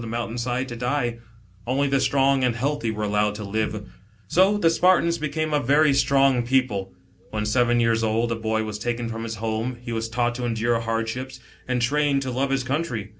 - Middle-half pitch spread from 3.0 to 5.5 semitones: Yes, average, 3.4 semitones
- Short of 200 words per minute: No, fast, 205 wpm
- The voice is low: Yes, low, 120 Hz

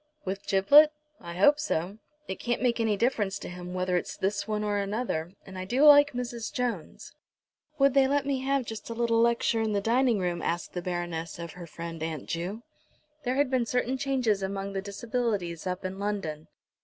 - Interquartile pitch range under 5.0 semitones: No, average, 5.3 semitones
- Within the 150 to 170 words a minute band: No, average, 200 wpm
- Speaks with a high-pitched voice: Yes, high, 205 Hz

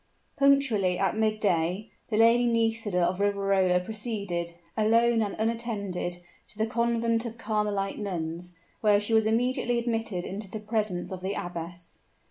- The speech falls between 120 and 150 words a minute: Yes, average, 140 wpm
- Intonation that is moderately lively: Yes, average, 3.6 semitones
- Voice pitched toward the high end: Yes, high, 210 Hz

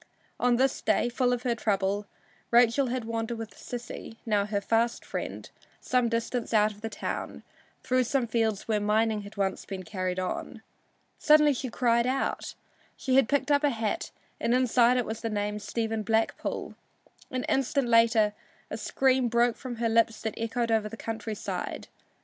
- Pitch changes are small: Yes, narrow, 2.3 semitones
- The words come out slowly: No, average, 175 wpm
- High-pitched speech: Yes, high, 230 Hz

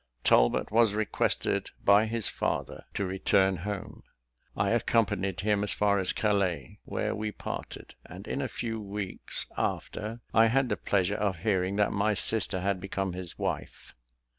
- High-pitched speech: No, low, 100 Hz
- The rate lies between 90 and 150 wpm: No, average, 160 wpm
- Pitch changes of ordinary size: No, narrow, 2.2 semitones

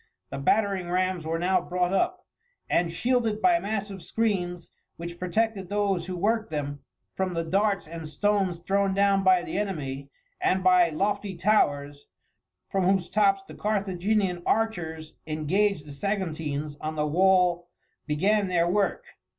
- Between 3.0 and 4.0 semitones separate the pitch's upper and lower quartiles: Yes, average, 3.3 semitones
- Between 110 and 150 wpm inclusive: Yes, average, 145 wpm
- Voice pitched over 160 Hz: Yes, medium, 185 Hz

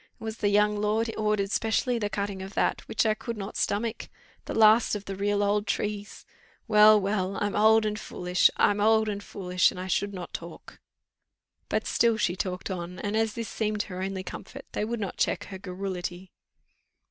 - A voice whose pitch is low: No, high, 205 Hz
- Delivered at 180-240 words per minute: Yes, average, 195 wpm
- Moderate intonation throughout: No, narrow, 2.0 semitones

